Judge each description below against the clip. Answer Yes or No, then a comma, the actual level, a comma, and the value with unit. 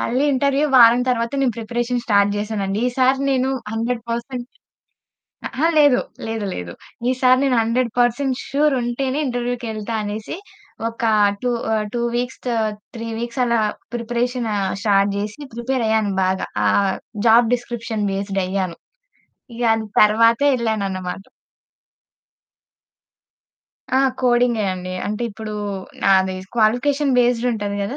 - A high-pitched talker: Yes, high, 235 Hz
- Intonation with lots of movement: No, average, 2.8 semitones